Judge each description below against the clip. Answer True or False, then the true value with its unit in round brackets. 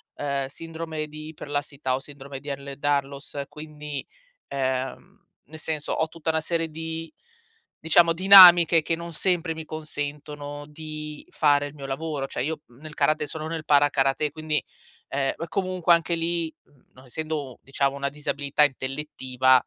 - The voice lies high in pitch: False (150 Hz)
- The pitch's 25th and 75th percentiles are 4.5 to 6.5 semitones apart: False (2.4 semitones)